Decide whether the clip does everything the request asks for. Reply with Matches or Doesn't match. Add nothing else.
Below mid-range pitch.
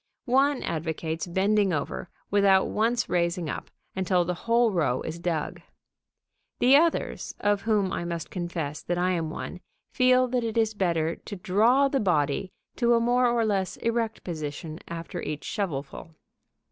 Doesn't match